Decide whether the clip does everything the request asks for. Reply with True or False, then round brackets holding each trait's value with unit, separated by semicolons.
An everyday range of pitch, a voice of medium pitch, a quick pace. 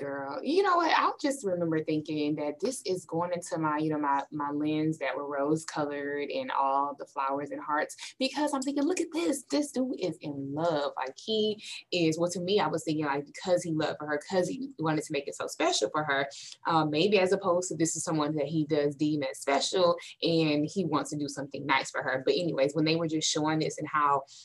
True (3.9 semitones; 155 Hz; 245 wpm)